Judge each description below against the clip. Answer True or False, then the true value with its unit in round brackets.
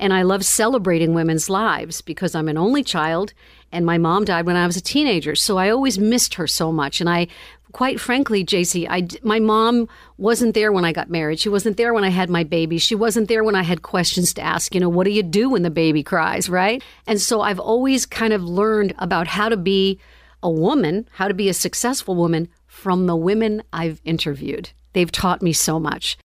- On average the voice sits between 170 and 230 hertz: True (185 Hz)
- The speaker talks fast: True (225 wpm)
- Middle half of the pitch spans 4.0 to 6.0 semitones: True (4.3 semitones)